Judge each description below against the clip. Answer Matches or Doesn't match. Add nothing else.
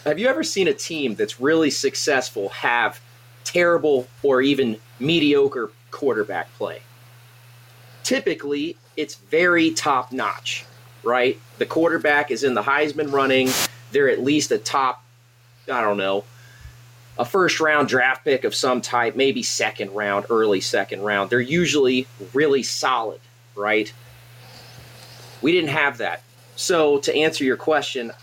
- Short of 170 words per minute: Matches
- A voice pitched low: Matches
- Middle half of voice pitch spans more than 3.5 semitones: Matches